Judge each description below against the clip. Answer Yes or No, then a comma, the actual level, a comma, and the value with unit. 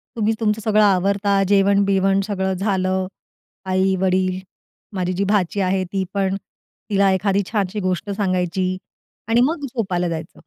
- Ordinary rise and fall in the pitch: No, narrow, 1.6 semitones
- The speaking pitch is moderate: No, high, 195 Hz